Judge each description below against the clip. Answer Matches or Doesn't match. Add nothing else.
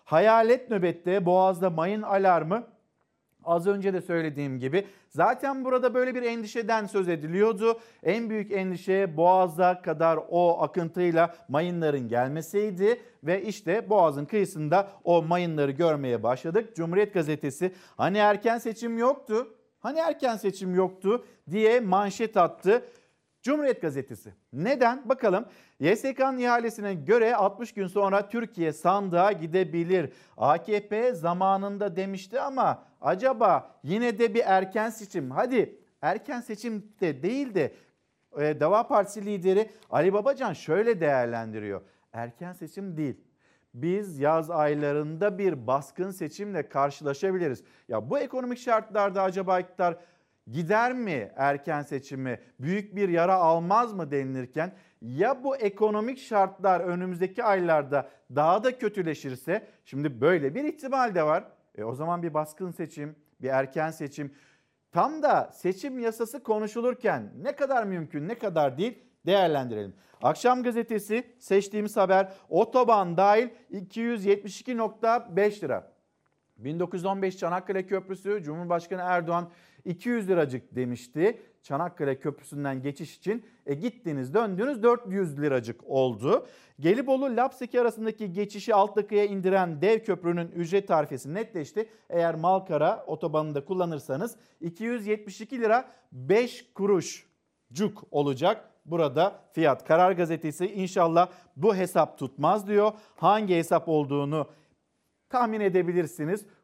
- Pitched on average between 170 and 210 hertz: Matches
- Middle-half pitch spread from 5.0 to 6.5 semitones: Matches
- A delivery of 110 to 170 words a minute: Matches